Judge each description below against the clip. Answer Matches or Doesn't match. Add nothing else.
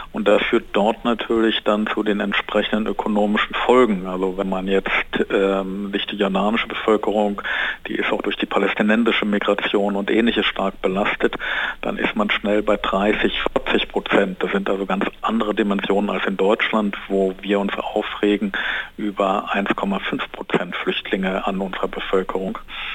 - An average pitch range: Doesn't match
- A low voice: Matches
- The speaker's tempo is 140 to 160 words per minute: Matches